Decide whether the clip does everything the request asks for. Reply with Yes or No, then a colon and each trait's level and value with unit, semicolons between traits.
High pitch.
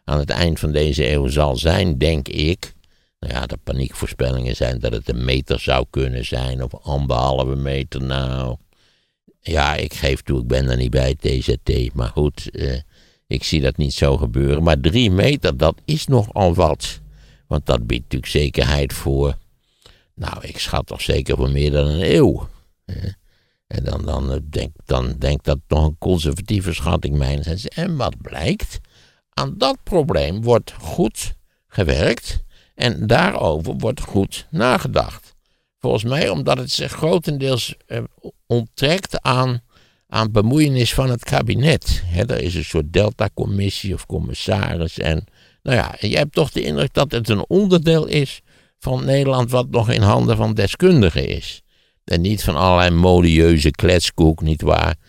No: very low, 80 Hz